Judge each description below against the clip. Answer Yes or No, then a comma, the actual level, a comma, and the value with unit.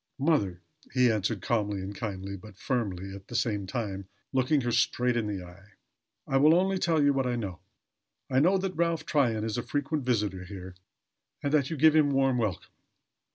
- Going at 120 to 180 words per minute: No, average, 195 wpm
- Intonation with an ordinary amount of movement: No, wide, 6.2 semitones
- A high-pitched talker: No, low, 120 Hz